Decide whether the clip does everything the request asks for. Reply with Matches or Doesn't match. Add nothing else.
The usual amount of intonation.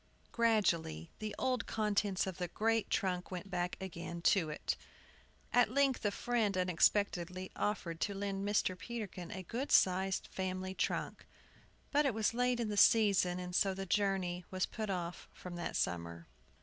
Matches